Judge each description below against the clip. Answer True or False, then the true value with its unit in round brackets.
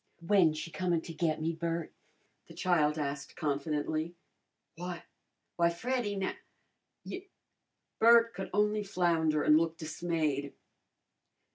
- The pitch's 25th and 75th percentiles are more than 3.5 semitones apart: False (3.2 semitones)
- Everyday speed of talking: False (125 wpm)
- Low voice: False (165 Hz)